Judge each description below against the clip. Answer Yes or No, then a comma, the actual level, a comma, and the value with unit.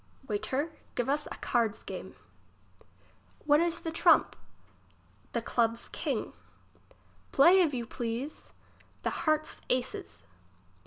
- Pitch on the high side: Yes, very high, 270 Hz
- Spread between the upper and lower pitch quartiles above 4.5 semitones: Yes, average, 5.0 semitones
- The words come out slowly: Yes, slow, 110 wpm